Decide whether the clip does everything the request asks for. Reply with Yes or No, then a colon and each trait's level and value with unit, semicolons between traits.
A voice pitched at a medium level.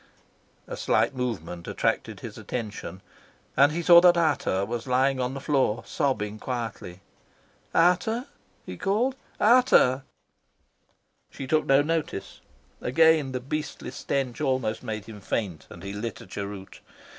No: low, 130 Hz